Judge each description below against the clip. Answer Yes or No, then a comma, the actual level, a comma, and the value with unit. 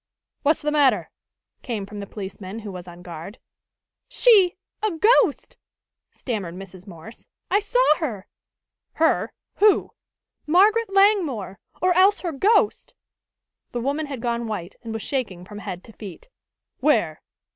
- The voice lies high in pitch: Yes, high, 240 Hz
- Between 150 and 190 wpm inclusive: No, average, 140 wpm